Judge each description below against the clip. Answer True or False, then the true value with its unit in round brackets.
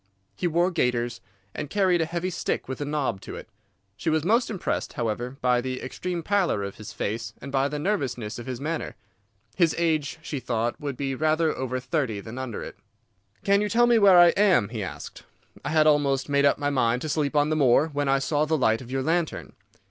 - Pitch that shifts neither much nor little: True (4.7 semitones)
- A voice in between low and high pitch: True (145 Hz)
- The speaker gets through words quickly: True (220 wpm)